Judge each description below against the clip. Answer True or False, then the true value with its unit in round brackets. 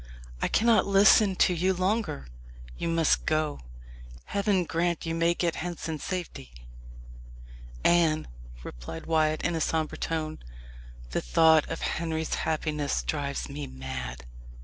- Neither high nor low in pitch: True (160 Hz)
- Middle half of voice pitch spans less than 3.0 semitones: True (2.6 semitones)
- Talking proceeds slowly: True (130 wpm)